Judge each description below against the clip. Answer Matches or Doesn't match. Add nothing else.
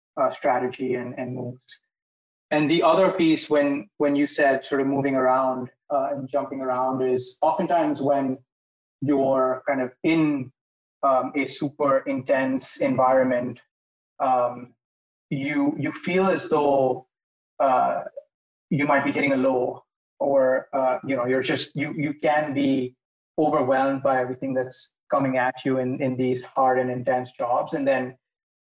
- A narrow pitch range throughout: Matches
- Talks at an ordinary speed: Matches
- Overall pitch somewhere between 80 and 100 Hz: Doesn't match